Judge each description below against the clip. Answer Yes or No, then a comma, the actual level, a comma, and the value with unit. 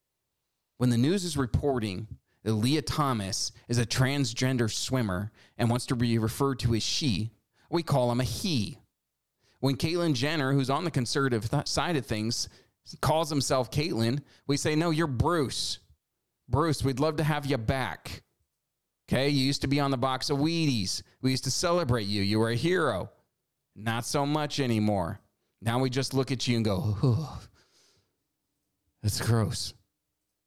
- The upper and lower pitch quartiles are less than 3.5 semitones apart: No, average, 3.8 semitones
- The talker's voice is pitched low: Yes, low, 130 Hz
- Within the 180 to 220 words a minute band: No, average, 165 wpm